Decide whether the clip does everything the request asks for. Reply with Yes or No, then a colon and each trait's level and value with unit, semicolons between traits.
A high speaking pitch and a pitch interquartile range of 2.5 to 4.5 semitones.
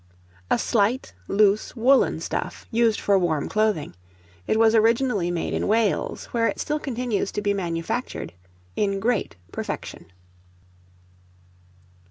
Yes: high, 215 Hz; average, 3.1 semitones